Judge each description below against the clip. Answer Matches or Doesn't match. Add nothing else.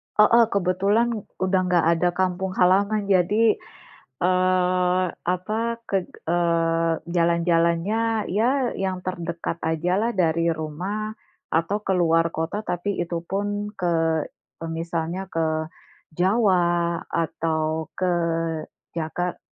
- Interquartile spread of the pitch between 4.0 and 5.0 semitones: Doesn't match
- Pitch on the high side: Doesn't match